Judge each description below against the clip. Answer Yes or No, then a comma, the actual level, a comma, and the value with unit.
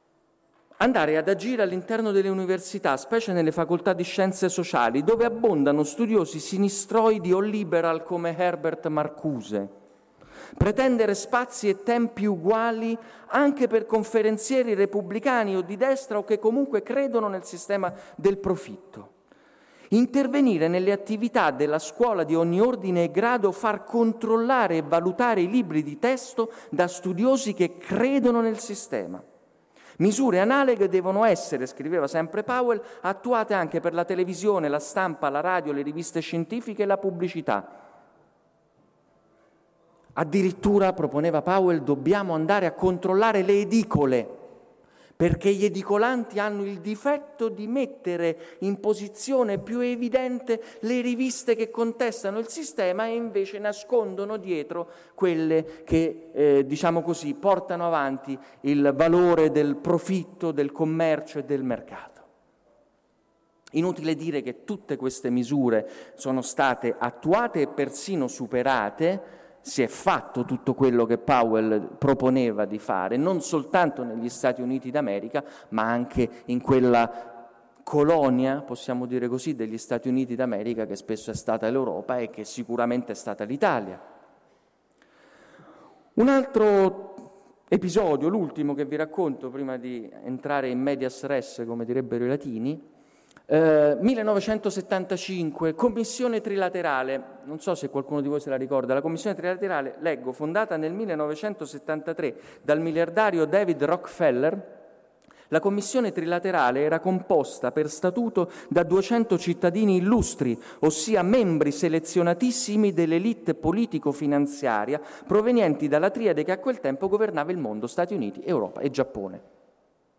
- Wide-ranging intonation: Yes, wide, 6.7 semitones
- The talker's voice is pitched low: No, medium, 180 Hz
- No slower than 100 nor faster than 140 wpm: Yes, average, 130 wpm